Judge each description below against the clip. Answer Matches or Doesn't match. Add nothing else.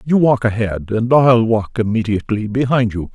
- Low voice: Matches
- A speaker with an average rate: Matches